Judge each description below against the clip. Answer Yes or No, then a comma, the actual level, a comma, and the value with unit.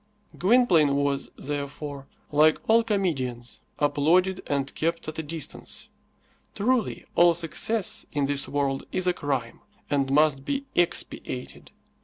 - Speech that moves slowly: Yes, slow, 125 wpm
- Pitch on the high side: No, medium, 150 Hz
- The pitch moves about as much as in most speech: Yes, average, 4.4 semitones